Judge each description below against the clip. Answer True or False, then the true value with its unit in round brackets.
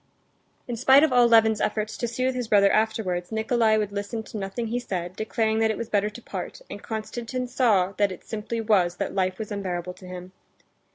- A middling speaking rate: False (210 wpm)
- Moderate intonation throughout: True (3.0 semitones)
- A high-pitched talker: True (220 Hz)